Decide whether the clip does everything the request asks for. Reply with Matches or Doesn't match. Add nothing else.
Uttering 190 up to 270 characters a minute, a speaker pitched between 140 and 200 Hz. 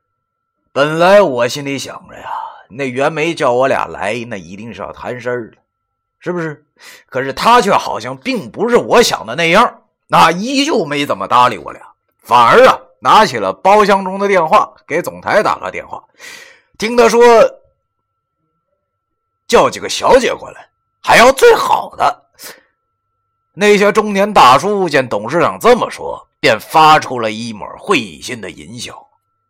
Matches